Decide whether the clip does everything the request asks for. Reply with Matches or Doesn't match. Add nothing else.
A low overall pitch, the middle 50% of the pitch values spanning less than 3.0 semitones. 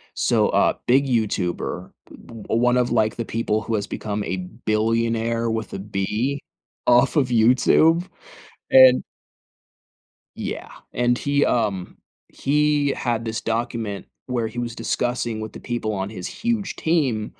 Matches